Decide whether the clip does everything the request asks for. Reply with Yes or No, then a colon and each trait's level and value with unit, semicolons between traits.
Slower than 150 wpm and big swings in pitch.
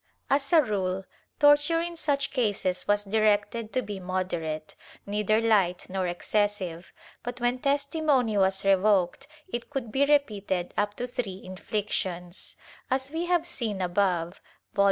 Yes: average, 140 wpm; wide, 6.1 semitones